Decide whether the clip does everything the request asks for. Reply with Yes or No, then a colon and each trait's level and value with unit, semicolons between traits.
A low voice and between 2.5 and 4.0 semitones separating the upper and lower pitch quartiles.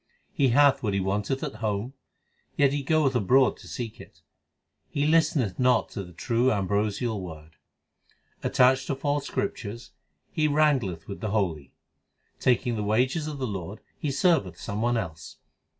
No: low, 120 Hz; average, 5.3 semitones